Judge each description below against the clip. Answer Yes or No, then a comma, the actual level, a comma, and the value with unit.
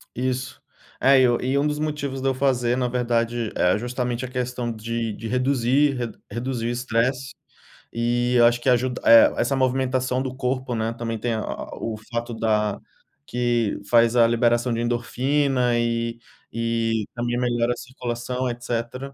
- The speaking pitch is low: Yes, low, 120 Hz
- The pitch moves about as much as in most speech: No, narrow, 1.6 semitones